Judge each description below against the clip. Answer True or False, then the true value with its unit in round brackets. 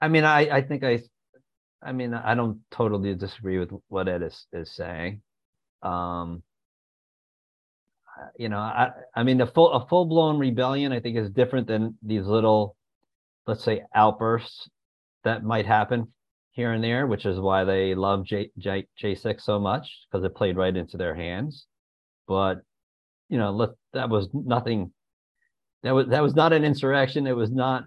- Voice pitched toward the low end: True (115 Hz)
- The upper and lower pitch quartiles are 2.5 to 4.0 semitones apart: False (4.7 semitones)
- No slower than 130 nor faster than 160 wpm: False (175 wpm)